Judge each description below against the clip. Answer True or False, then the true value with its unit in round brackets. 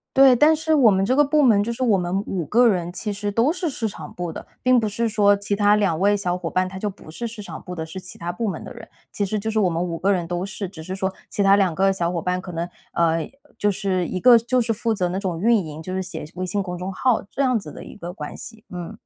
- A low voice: False (195 Hz)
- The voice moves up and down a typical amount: True (4.0 semitones)